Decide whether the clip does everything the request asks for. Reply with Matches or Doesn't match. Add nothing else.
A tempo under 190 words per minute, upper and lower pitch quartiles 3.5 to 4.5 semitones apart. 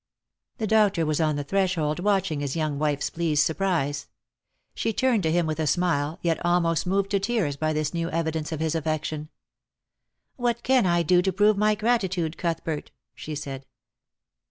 Matches